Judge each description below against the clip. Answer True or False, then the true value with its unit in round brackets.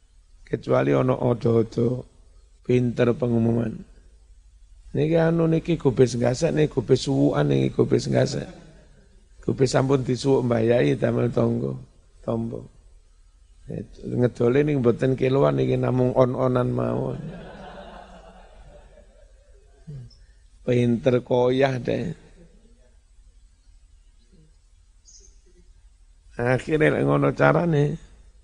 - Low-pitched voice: True (115 Hz)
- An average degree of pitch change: False (8.7 semitones)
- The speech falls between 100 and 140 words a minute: False (85 wpm)